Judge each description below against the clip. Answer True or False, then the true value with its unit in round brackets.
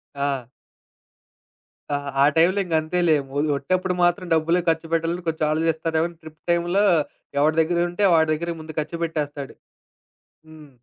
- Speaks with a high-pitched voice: False (165 Hz)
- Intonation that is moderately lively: False (1.7 semitones)